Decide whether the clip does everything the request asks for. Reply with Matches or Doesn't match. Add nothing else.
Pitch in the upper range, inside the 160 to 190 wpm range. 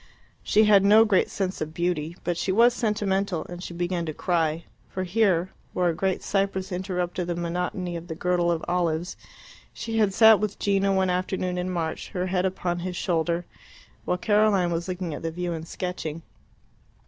Doesn't match